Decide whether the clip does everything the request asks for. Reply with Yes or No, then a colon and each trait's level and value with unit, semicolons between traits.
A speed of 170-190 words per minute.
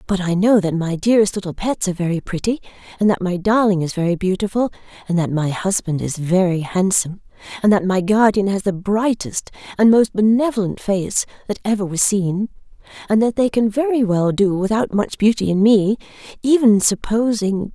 Yes: average, 180 wpm